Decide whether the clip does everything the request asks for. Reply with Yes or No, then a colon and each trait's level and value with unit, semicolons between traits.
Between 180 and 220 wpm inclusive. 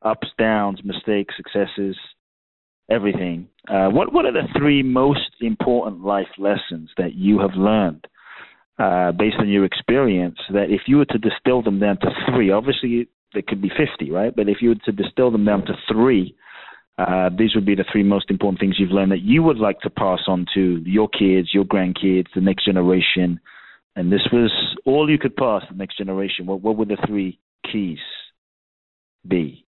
Yes: average, 190 wpm